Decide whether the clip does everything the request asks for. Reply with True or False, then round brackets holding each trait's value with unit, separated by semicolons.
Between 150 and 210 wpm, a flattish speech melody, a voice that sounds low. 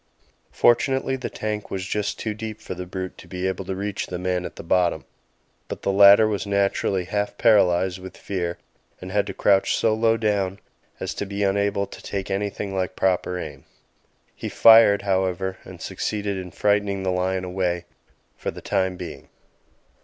True (180 wpm; 1.8 semitones; 95 Hz)